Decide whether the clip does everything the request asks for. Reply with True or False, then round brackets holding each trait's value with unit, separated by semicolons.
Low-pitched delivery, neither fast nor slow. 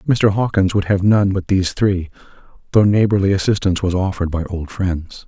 True (95 Hz; 180 wpm)